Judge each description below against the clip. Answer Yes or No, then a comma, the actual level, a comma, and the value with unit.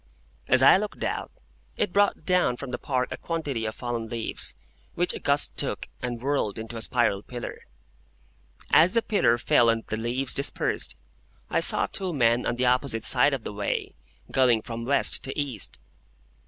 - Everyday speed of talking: Yes, average, 180 wpm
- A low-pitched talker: Yes, low, 125 Hz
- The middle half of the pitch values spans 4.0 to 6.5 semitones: No, average, 3.6 semitones